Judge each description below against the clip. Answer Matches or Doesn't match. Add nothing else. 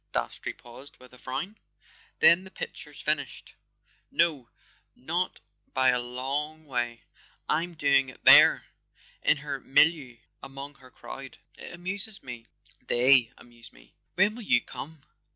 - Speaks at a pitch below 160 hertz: Matches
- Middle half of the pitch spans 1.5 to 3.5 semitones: Doesn't match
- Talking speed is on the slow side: Matches